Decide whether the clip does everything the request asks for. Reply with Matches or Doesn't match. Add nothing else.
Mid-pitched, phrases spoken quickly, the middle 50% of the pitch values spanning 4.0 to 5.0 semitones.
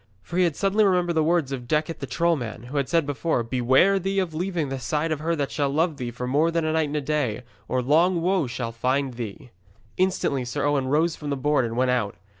Matches